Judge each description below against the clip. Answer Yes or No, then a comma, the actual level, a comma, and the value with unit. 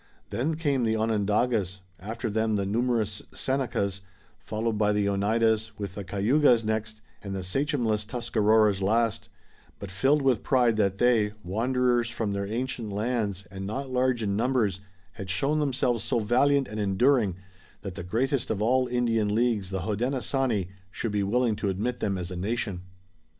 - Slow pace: No, average, 160 wpm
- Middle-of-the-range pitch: No, low, 110 Hz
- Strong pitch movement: No, average, 3.5 semitones